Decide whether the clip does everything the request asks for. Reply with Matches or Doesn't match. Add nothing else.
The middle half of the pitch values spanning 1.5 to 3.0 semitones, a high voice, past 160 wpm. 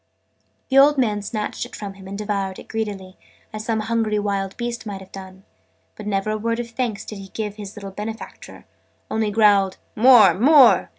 Matches